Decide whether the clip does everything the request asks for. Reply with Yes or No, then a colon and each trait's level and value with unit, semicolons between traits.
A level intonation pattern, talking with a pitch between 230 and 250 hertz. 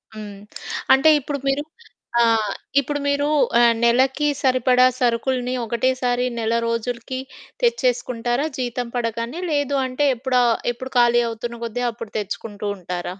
Yes: narrow, 2.2 semitones; high, 245 Hz